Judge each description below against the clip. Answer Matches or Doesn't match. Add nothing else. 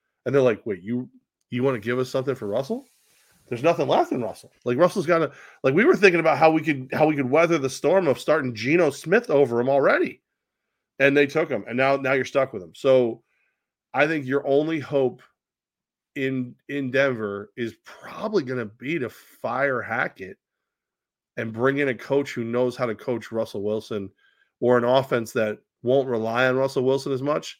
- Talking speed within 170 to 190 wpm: Doesn't match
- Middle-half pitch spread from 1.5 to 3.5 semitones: Matches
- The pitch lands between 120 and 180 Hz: Matches